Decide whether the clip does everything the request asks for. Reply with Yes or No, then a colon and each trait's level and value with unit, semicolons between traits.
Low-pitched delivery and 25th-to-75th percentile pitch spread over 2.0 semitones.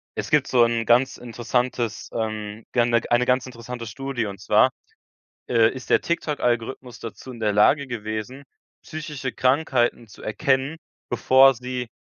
Yes: low, 125 Hz; narrow, 2.5 semitones